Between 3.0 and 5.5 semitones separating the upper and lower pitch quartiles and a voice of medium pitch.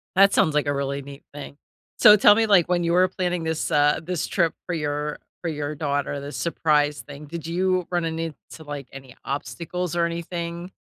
Yes: average, 3.3 semitones; medium, 160 Hz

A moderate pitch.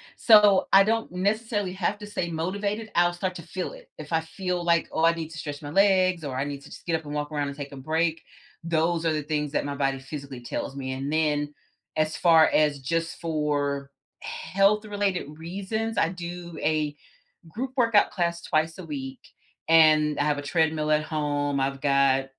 Yes: medium, 160 Hz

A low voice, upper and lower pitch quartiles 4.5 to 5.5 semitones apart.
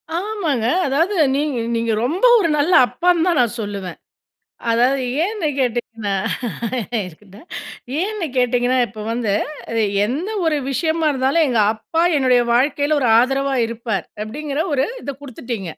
No: very high, 260 Hz; average, 5.1 semitones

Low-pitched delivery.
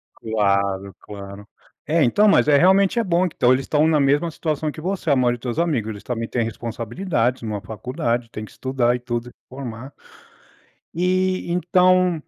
Yes: low, 130 Hz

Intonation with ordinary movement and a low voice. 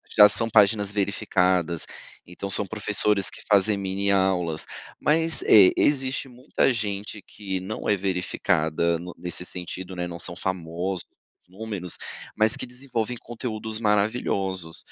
Yes: average, 3.2 semitones; low, 100 Hz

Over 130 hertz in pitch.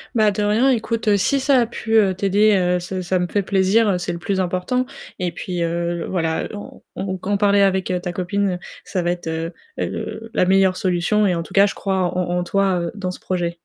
Yes: high, 190 Hz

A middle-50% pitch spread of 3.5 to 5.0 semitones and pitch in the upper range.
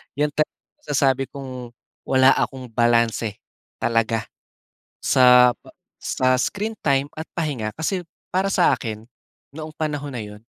No: average, 4.3 semitones; low, 130 Hz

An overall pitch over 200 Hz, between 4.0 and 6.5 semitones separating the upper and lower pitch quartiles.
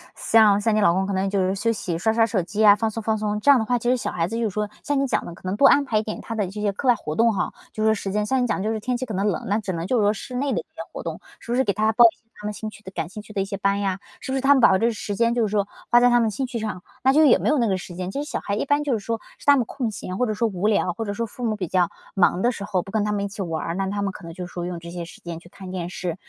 No: high, 210 Hz; average, 3.3 semitones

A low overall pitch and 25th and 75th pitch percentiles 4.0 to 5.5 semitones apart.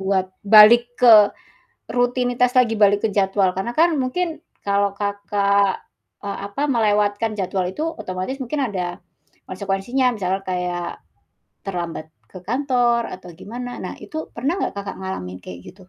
No: high, 205 Hz; average, 4.4 semitones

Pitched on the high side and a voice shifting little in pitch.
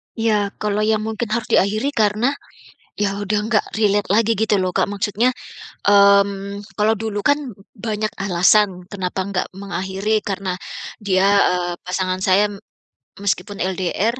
Yes: high, 205 Hz; narrow, 2.0 semitones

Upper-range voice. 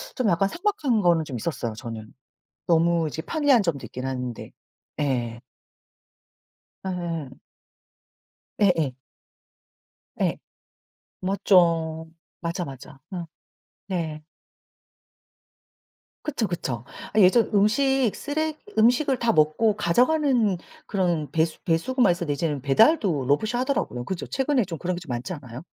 No: medium, 175 Hz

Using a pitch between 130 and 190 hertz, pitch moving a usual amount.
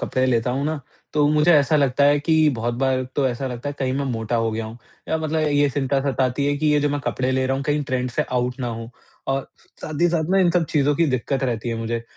Yes: low, 135 Hz; average, 3.0 semitones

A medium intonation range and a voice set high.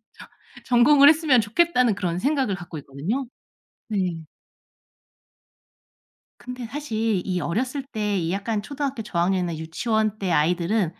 No: wide, 6.1 semitones; high, 215 Hz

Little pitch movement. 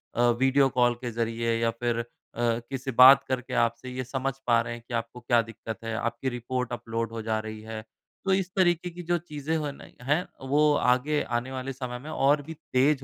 No: average, 3.1 semitones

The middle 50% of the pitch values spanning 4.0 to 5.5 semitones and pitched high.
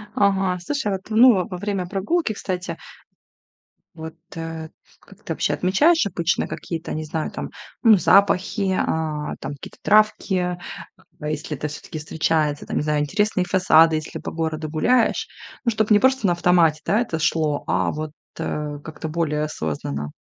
No: average, 4.5 semitones; medium, 170 Hz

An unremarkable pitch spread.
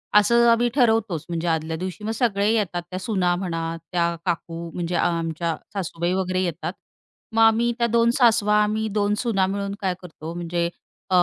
Yes: average, 4.2 semitones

